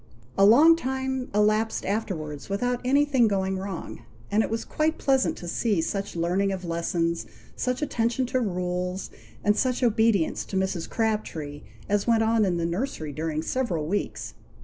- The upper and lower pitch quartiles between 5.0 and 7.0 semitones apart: Yes, wide, 5.5 semitones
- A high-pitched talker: Yes, high, 205 Hz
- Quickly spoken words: No, average, 160 wpm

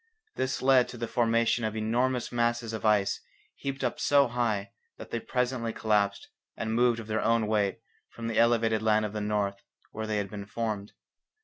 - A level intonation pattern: Yes, narrow, 1.9 semitones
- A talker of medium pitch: No, low, 115 Hz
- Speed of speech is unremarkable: Yes, average, 190 wpm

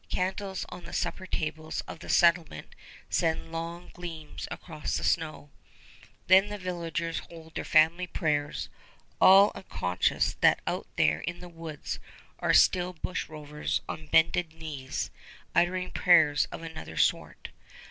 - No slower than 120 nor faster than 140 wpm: Yes, slow, 135 wpm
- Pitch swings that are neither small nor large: No, narrow, 2.3 semitones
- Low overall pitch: No, medium, 165 Hz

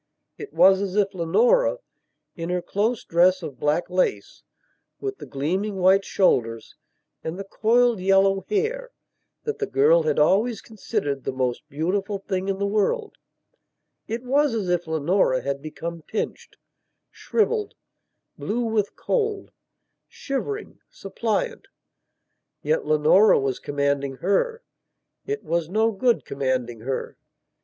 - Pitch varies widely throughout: Yes, wide, 8.3 semitones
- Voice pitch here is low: No, high, 195 Hz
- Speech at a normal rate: No, slow, 130 wpm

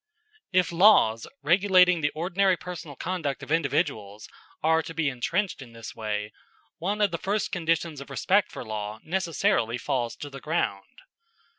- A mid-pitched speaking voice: Yes, medium, 160 Hz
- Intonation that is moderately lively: No, wide, 6.5 semitones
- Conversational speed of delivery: Yes, average, 155 wpm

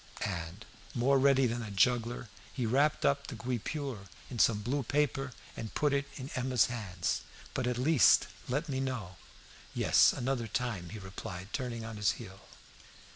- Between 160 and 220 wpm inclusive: Yes, average, 170 wpm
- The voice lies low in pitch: Yes, low, 120 Hz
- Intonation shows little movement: No, average, 4.2 semitones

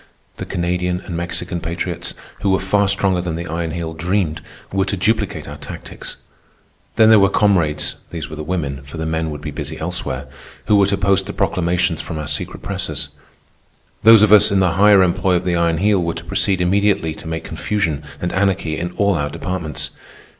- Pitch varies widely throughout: No, average, 3.3 semitones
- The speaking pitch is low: Yes, very low, 90 Hz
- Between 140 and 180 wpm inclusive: No, average, 200 wpm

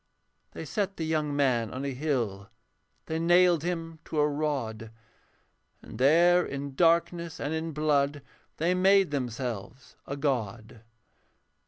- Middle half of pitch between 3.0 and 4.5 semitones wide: Yes, average, 4.2 semitones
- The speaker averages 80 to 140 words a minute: Yes, slow, 135 wpm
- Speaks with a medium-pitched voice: Yes, medium, 150 Hz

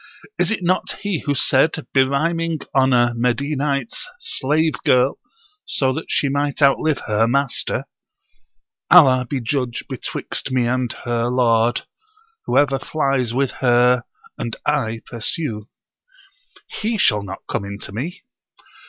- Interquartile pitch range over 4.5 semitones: No, average, 3.5 semitones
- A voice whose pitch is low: Yes, low, 130 Hz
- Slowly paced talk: Yes, slow, 130 wpm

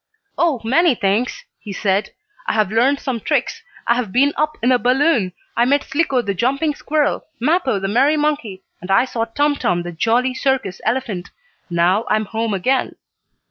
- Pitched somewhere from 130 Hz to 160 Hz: No, high, 245 Hz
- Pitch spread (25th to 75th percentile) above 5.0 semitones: Yes, wide, 5.5 semitones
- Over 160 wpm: Yes, average, 180 wpm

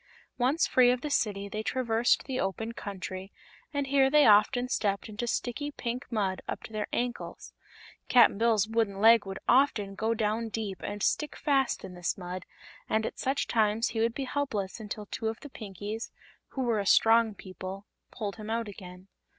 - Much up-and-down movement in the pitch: No, average, 3.4 semitones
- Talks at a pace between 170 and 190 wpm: Yes, average, 185 wpm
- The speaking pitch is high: Yes, high, 225 Hz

